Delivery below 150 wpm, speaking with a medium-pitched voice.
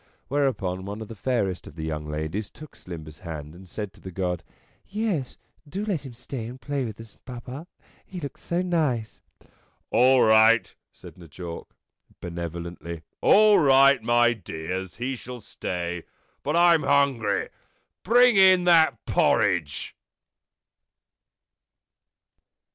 No: average, 140 wpm; low, 115 Hz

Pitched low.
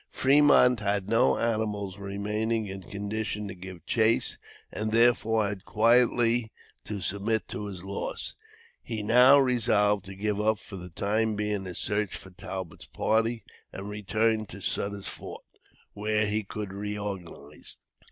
Yes: low, 105 Hz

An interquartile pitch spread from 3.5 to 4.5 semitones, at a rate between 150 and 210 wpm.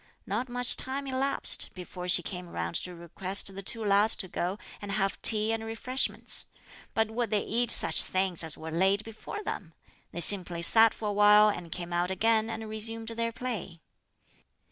Yes: average, 3.9 semitones; average, 185 wpm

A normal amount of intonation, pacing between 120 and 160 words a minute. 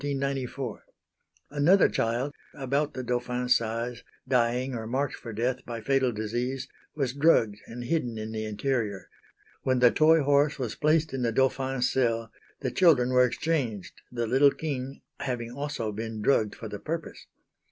Yes: average, 3.2 semitones; average, 150 wpm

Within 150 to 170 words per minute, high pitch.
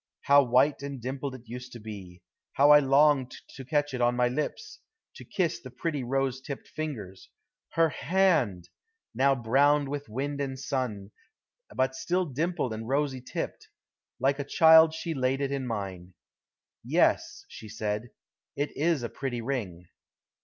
No: average, 160 wpm; low, 135 Hz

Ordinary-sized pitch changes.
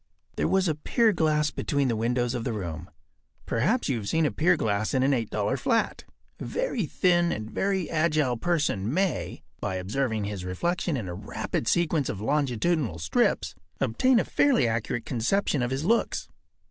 No: wide, 7.6 semitones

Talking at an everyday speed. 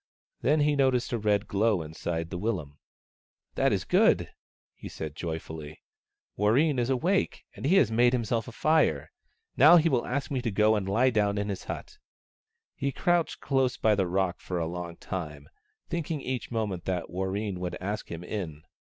Yes: average, 185 wpm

